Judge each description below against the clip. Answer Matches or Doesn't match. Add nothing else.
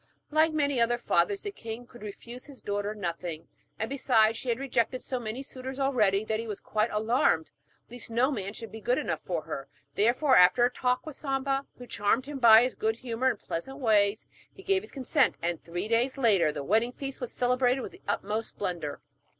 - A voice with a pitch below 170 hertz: Doesn't match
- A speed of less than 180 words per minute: Doesn't match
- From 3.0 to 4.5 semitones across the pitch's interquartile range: Matches